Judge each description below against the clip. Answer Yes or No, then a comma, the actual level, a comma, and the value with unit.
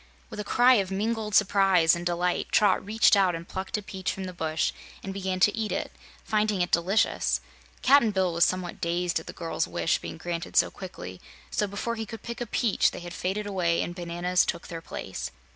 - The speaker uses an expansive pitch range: No, average, 3.3 semitones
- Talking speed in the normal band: No, fast, 210 wpm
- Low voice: No, medium, 185 Hz